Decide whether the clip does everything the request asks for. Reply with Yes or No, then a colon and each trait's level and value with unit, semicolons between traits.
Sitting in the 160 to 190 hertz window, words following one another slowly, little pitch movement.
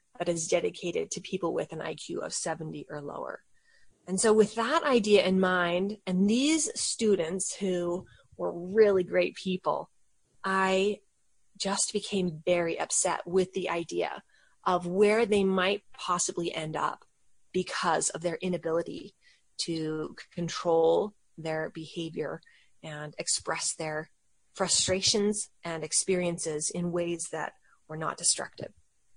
No: medium, 185 Hz; slow, 130 wpm; average, 3.1 semitones